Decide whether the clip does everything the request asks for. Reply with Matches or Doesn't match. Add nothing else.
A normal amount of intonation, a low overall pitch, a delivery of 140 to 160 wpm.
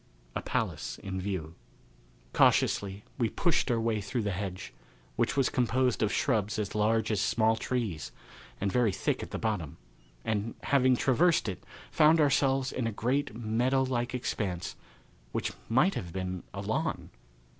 Matches